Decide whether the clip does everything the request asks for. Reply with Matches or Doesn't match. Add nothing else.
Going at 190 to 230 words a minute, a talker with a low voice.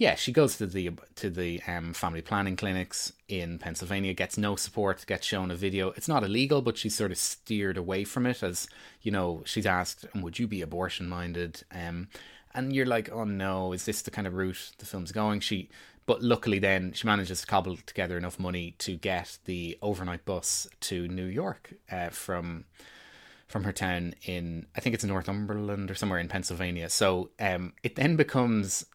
Matches